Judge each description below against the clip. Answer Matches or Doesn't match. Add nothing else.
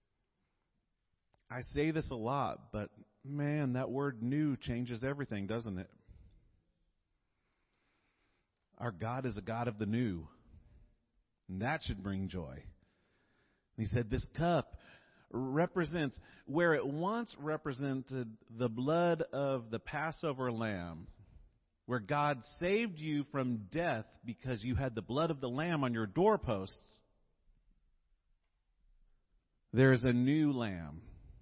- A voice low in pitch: Matches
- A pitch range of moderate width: Doesn't match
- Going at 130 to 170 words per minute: Doesn't match